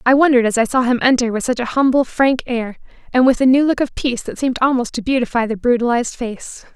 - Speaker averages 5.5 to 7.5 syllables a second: Yes, 6.5 syllables/s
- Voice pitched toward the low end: No, high, 245 Hz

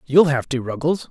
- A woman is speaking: No, male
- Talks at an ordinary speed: No, fast, 215 wpm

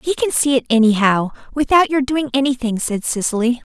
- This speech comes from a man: No, female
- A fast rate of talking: No, average, 180 wpm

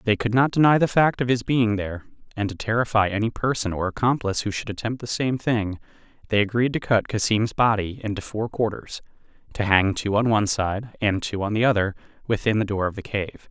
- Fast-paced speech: Yes, fast, 215 wpm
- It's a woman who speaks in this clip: No, male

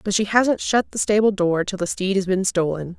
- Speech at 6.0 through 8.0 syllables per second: No, 5.2 syllables/s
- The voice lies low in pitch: No, high, 195 Hz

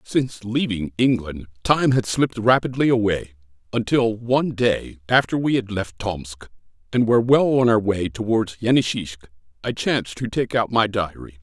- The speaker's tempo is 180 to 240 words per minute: No, average, 165 wpm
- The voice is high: No, low, 110 Hz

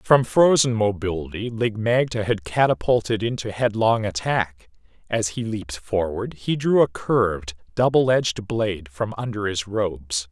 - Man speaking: Yes, male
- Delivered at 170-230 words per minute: No, average, 145 wpm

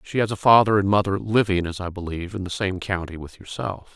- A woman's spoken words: No, male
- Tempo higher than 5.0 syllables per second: Yes, 6.0 syllables/s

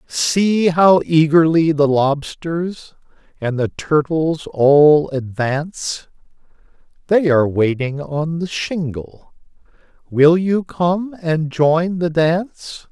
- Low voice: No, medium, 160 Hz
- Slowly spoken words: Yes, slow, 100 wpm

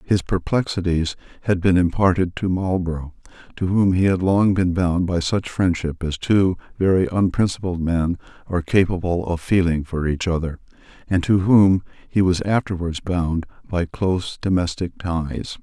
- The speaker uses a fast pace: No, average, 155 wpm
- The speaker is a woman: No, male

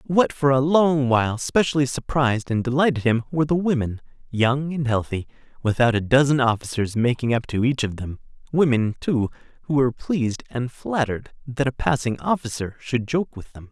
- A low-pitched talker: Yes, low, 130 Hz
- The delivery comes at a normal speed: Yes, average, 180 wpm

